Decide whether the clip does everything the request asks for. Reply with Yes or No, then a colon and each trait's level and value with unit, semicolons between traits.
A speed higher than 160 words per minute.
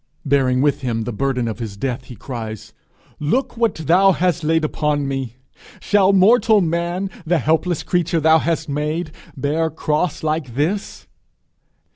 No: average, 150 wpm